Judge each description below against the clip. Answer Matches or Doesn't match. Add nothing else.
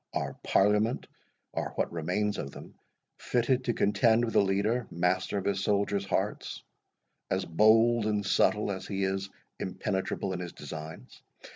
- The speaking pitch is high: Doesn't match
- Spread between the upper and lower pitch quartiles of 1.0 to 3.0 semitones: Matches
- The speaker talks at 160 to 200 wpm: Doesn't match